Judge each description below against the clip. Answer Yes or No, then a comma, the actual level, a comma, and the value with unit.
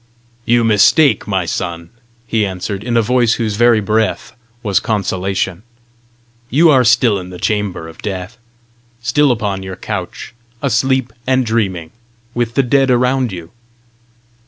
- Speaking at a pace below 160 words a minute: Yes, average, 140 wpm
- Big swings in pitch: No, average, 4.2 semitones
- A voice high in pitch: No, low, 110 Hz